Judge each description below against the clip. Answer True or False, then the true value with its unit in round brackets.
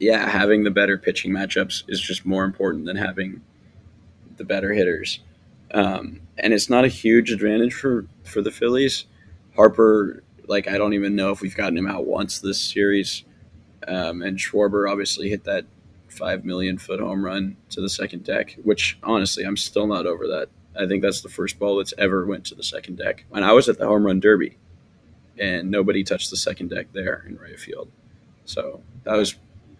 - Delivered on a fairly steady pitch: True (1.7 semitones)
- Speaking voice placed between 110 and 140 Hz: False (100 Hz)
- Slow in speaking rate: False (190 wpm)